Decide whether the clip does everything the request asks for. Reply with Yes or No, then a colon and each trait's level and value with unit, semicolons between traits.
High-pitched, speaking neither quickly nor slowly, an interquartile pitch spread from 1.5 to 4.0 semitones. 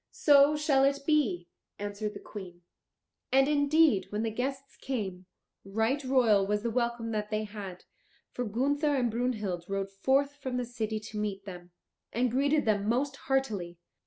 No: high, 230 Hz; average, 160 wpm; average, 4.9 semitones